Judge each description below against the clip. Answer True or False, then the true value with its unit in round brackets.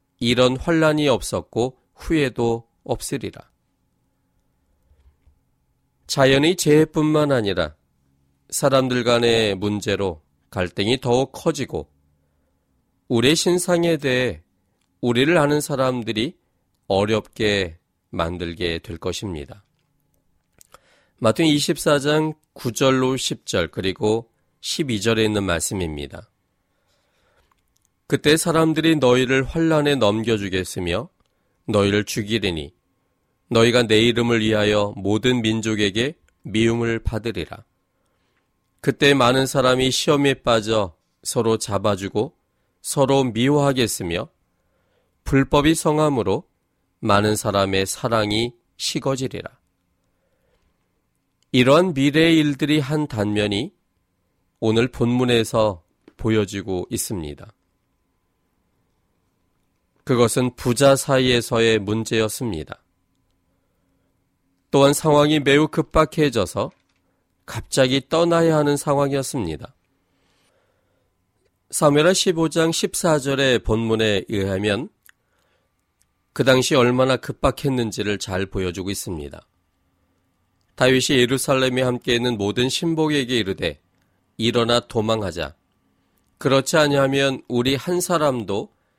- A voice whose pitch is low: True (115 Hz)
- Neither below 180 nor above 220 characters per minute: True (215 characters per minute)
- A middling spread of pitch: False (6.1 semitones)